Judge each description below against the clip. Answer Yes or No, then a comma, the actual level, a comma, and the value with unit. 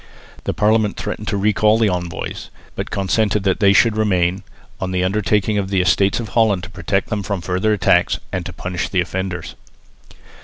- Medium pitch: No, low, 100 Hz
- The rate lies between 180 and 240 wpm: Yes, average, 185 wpm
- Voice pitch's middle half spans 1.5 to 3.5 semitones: Yes, narrow, 2.5 semitones